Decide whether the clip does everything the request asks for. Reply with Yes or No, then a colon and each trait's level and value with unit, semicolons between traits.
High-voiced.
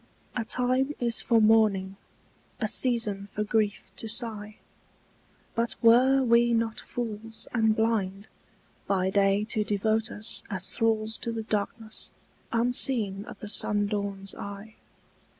Yes: high, 220 Hz